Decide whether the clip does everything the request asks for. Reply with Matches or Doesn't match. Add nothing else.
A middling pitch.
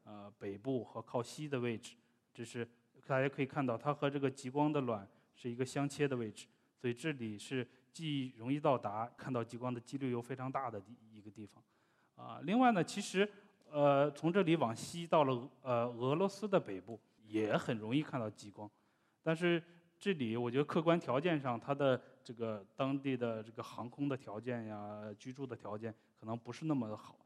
Doesn't match